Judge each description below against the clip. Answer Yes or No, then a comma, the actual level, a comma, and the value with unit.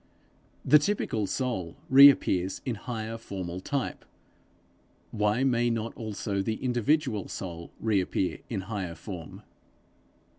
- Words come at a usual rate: No, slow, 110 wpm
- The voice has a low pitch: Yes, low, 110 Hz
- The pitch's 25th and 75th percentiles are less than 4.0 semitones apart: No, average, 4.5 semitones